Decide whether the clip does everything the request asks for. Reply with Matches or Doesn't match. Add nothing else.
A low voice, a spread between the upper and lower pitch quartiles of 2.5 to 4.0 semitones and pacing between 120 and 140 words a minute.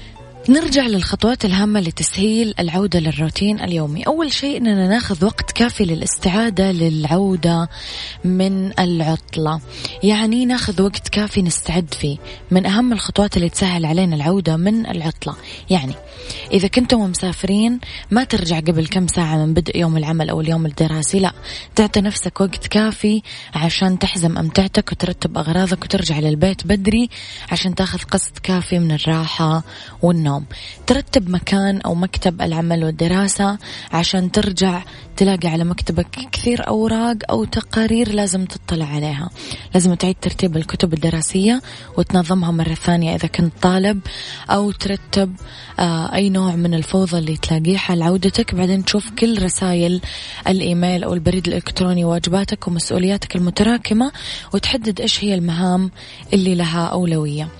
Doesn't match